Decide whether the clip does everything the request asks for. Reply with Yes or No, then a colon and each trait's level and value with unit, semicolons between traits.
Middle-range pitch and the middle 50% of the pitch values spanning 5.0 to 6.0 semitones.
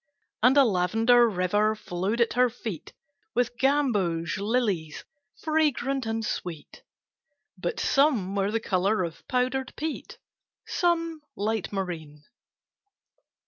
No: high, 220 Hz; wide, 5.6 semitones